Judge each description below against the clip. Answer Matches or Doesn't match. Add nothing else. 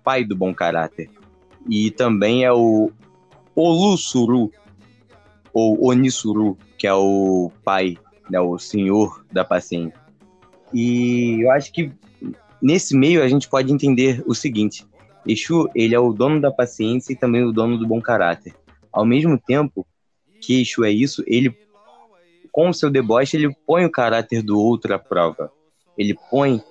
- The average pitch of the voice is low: Matches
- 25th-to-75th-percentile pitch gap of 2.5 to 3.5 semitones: Doesn't match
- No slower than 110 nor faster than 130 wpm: Doesn't match